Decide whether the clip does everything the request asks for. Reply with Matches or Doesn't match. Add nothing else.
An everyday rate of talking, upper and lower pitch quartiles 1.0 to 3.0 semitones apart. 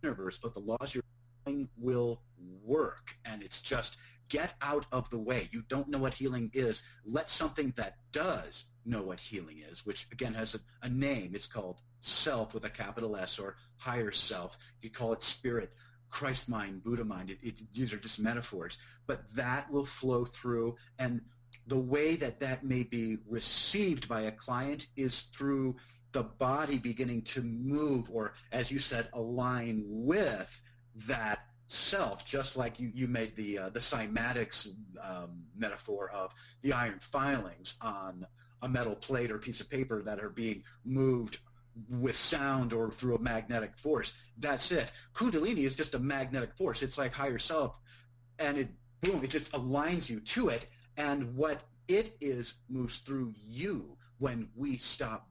Matches